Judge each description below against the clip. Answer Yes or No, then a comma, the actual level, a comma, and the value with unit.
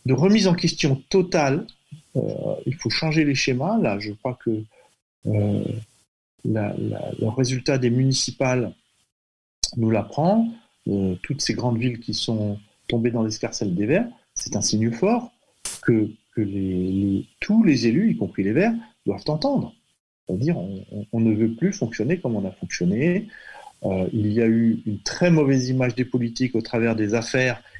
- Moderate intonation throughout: No, wide, 5.9 semitones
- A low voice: Yes, low, 120 Hz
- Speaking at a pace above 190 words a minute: No, average, 175 wpm